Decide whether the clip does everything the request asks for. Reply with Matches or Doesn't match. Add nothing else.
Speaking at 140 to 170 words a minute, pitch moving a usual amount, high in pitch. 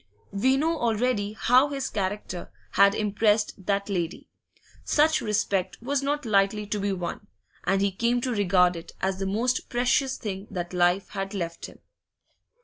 Matches